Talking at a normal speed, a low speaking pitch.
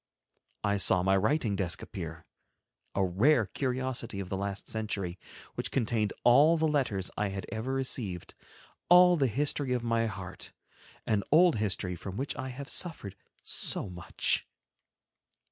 Yes: average, 145 wpm; low, 110 Hz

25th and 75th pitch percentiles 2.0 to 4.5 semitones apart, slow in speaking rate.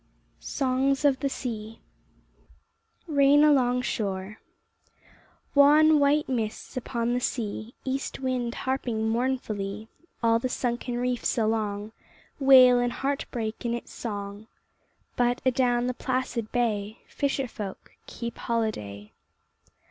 Yes: average, 3.1 semitones; slow, 115 wpm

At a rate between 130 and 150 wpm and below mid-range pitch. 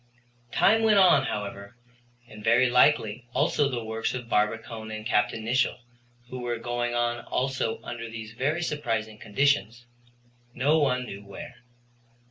Yes: average, 140 wpm; low, 120 Hz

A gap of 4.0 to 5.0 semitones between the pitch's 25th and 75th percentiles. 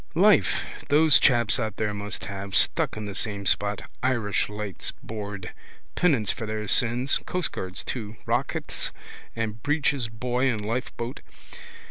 No: average, 3.4 semitones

